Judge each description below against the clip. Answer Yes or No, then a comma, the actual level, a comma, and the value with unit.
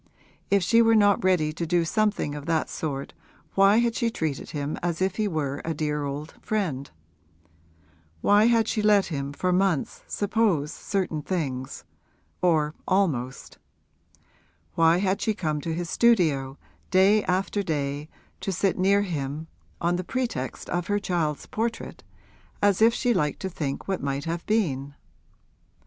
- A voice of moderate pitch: Yes, medium, 175 Hz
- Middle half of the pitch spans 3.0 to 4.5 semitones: No, average, 5.3 semitones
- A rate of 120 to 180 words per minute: Yes, average, 155 wpm